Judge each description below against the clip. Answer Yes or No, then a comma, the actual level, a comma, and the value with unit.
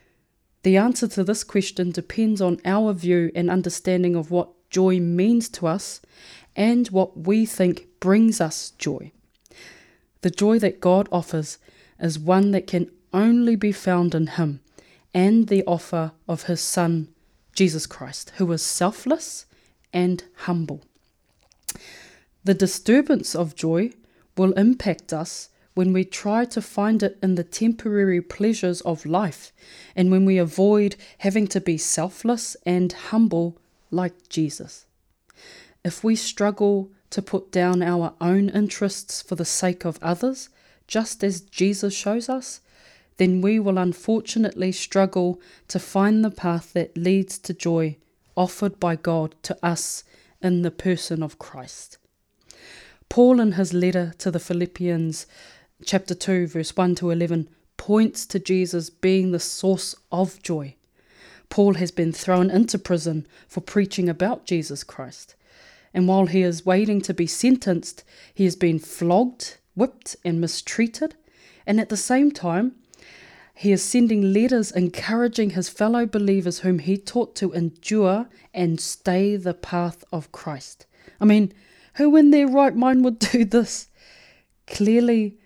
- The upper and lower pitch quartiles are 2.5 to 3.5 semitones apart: Yes, average, 3.1 semitones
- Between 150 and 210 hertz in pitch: Yes, medium, 185 Hz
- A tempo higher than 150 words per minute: No, average, 145 wpm